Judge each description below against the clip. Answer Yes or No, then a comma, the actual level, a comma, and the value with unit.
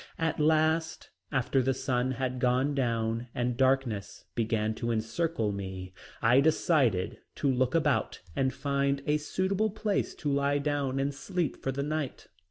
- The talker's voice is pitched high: No, low, 135 Hz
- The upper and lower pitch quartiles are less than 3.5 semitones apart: No, average, 3.8 semitones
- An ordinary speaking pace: Yes, average, 155 wpm